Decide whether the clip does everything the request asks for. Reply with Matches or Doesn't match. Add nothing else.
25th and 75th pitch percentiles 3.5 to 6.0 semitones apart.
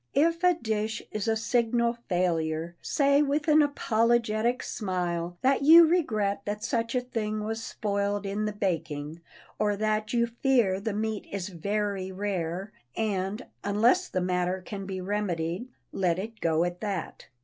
Matches